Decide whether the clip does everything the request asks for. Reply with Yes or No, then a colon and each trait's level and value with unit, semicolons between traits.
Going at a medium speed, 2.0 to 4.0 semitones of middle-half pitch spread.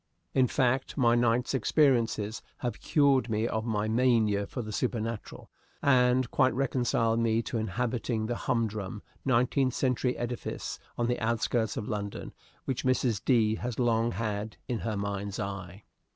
Yes: average, 150 wpm; narrow, 2.5 semitones